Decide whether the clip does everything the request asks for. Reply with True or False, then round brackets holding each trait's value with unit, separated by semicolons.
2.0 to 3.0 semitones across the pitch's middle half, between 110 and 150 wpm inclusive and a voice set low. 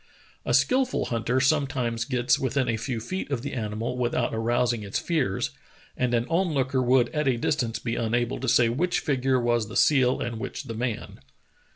False (2.6 semitones; 190 wpm; 125 Hz)